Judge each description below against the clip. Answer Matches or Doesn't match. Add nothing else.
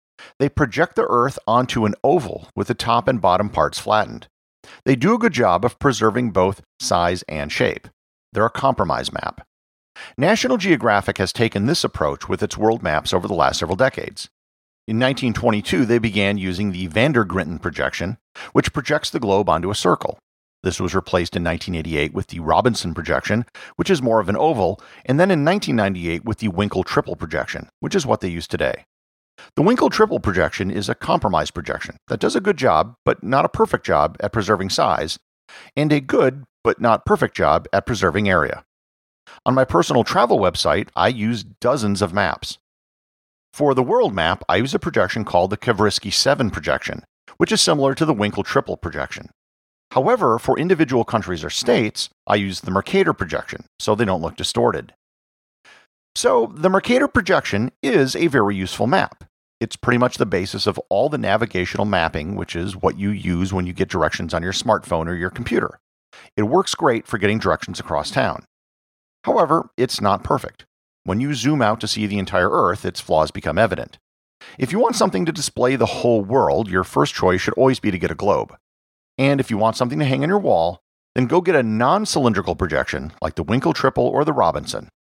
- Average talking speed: Matches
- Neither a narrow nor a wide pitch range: Doesn't match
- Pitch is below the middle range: Matches